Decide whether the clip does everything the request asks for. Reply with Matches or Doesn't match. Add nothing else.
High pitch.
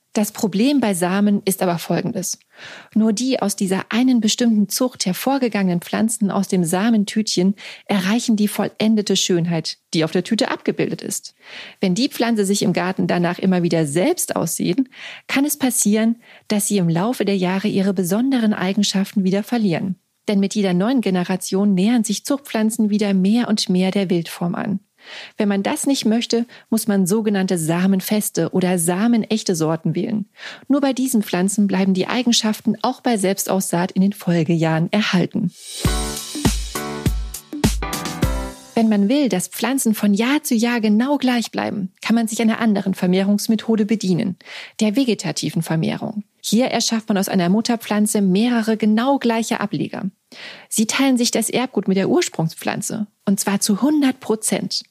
Matches